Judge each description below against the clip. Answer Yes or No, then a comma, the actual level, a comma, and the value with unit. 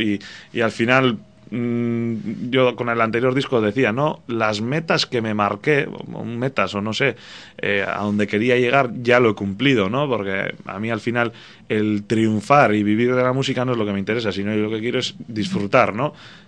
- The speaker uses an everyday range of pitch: Yes, average, 3.3 semitones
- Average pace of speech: No, fast, 210 wpm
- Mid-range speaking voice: No, low, 115 Hz